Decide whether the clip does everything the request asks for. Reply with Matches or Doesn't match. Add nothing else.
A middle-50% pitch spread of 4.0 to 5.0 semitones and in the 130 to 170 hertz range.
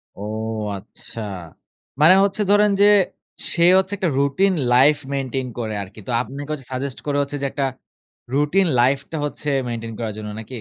Matches